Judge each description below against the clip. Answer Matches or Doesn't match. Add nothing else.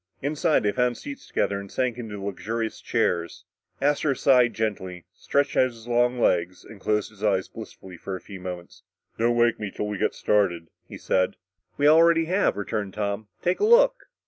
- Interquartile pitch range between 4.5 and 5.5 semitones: Matches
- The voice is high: Doesn't match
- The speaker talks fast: Doesn't match